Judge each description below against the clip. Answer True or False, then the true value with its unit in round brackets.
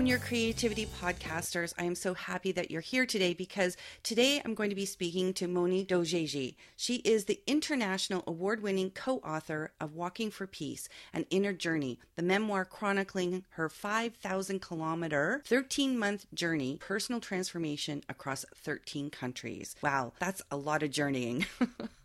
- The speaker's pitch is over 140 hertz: True (185 Hz)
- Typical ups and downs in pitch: True (4.5 semitones)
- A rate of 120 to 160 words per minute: True (145 wpm)